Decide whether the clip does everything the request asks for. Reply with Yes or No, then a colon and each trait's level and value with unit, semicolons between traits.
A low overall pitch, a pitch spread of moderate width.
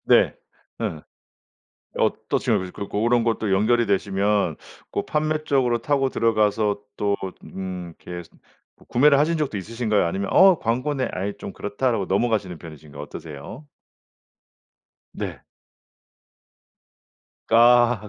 Yes: low, 110 Hz; average, 4.2 semitones